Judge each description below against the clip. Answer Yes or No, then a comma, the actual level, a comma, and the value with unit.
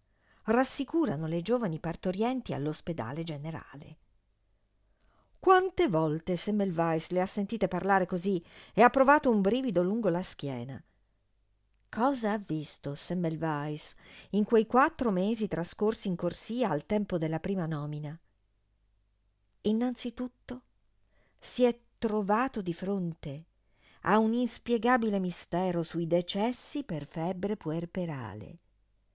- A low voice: No, medium, 175 Hz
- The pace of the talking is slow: Yes, slow, 110 wpm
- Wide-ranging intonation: Yes, wide, 6.9 semitones